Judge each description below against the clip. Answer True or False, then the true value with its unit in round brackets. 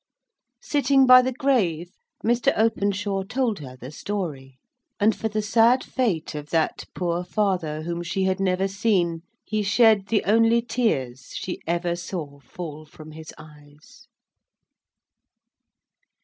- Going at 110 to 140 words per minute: True (135 wpm)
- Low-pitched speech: False (190 Hz)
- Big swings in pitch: True (5.8 semitones)